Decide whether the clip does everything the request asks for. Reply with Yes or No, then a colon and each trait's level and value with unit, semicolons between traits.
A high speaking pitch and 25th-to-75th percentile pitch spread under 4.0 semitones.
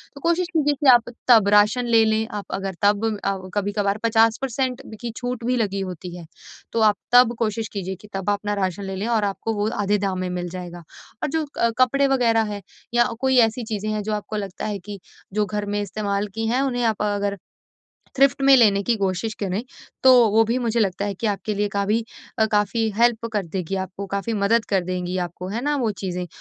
Yes: high, 210 Hz; average, 2.9 semitones